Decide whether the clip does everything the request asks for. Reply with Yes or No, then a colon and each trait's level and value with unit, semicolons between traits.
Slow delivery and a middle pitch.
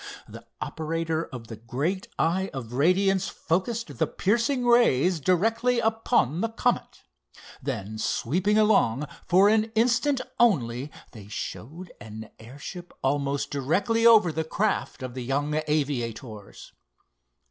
Yes: slow, 125 wpm; medium, 165 Hz